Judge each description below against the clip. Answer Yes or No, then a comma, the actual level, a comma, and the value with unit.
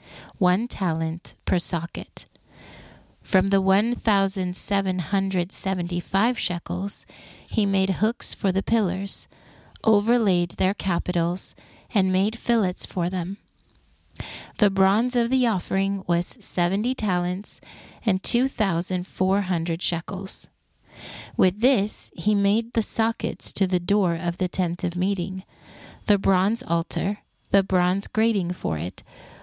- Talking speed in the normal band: No, slow, 130 wpm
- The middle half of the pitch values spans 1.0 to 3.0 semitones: Yes, average, 2.7 semitones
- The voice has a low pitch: No, high, 190 Hz